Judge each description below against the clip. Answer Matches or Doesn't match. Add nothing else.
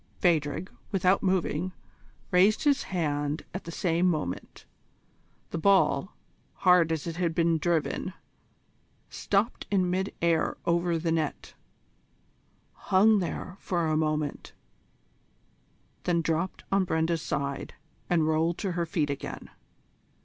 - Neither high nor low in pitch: Matches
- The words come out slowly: Matches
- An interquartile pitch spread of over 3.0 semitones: Doesn't match